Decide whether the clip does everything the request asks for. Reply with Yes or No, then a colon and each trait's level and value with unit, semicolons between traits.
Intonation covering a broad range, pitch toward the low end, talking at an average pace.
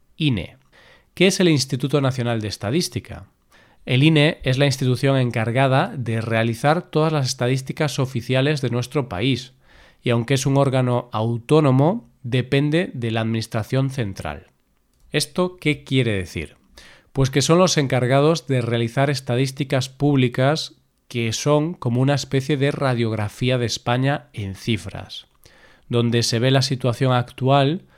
No: average, 3.4 semitones; low, 130 Hz; average, 135 wpm